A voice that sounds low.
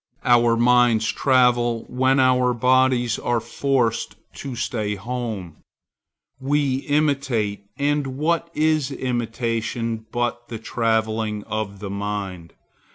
Yes: low, 120 Hz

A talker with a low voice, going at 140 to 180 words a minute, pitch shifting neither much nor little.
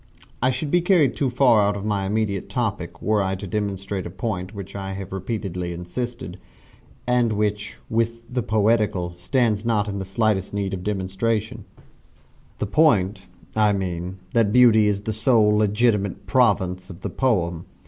Yes: low, 105 Hz; average, 170 wpm; average, 3.1 semitones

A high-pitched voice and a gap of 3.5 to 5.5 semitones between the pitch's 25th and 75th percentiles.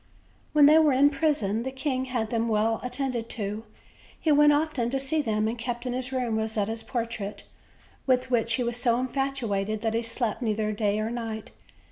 No: high, 235 Hz; average, 3.1 semitones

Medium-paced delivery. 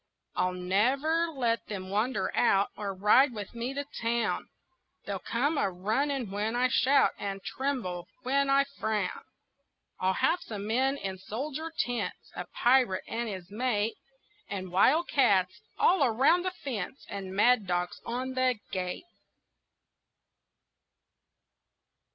No: slow, 130 wpm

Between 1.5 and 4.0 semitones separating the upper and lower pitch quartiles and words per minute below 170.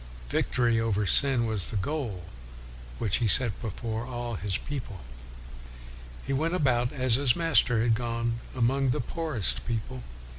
Yes: average, 3.1 semitones; average, 150 wpm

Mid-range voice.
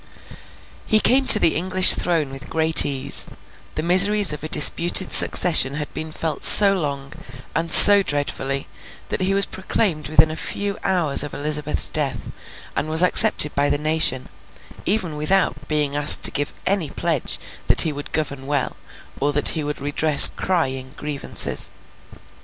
Yes: medium, 155 Hz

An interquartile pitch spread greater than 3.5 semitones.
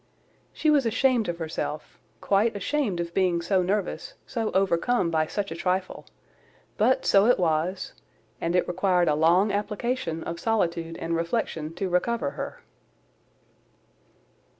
Yes: average, 4.6 semitones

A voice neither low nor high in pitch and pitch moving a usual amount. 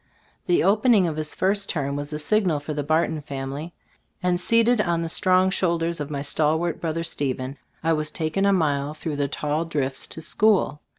Yes: medium, 160 Hz; average, 3.6 semitones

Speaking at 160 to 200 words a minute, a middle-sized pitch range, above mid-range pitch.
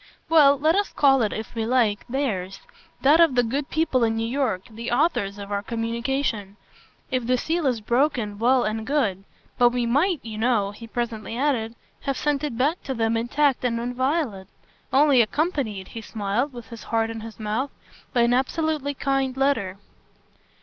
Yes: average, 180 wpm; average, 3.8 semitones; high, 240 Hz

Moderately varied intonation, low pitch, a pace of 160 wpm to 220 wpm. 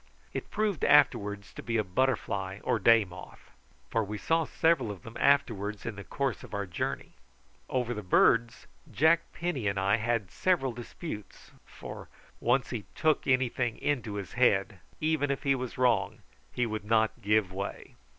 Yes: average, 4.7 semitones; low, 115 Hz; average, 170 wpm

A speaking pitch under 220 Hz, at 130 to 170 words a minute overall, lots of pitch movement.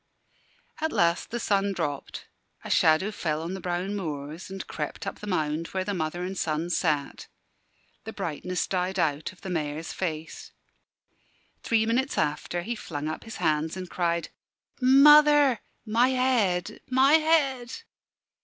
Yes: medium, 185 Hz; average, 150 wpm; wide, 6.2 semitones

